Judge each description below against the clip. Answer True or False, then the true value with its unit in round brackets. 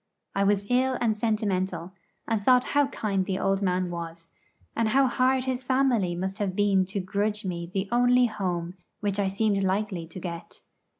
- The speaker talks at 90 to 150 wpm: False (180 wpm)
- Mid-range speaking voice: False (200 Hz)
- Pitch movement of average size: True (4.1 semitones)